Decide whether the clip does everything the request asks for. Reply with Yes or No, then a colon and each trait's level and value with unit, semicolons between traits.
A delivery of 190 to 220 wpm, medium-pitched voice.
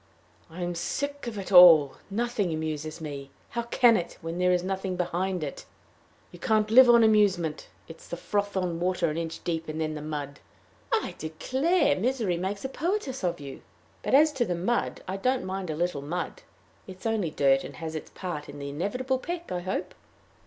Yes: average, 200 wpm; medium, 180 Hz